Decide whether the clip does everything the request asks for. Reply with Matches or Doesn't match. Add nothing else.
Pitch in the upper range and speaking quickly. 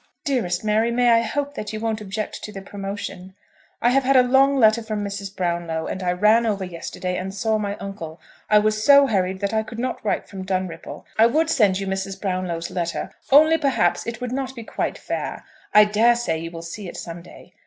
Matches